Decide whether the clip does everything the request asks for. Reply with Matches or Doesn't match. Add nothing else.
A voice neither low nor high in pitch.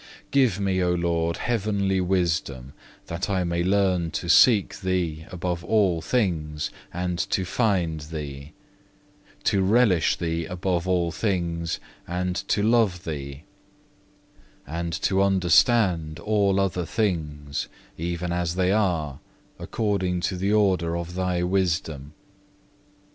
Doesn't match